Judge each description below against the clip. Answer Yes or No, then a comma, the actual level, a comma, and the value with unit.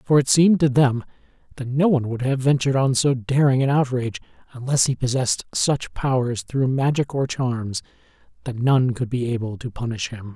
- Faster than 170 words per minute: Yes, average, 190 wpm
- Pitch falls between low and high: No, low, 130 Hz